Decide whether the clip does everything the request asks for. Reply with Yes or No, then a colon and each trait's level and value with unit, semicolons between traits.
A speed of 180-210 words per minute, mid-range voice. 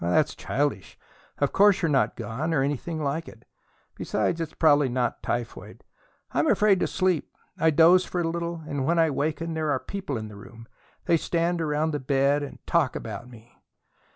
Yes: average, 185 wpm; medium, 150 Hz